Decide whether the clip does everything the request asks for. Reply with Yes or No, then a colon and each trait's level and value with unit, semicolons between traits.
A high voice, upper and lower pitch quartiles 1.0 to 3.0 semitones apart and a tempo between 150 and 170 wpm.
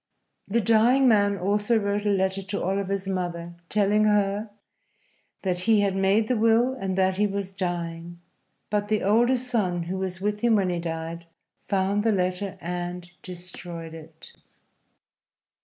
Yes: high, 195 Hz; average, 2.7 semitones; average, 155 wpm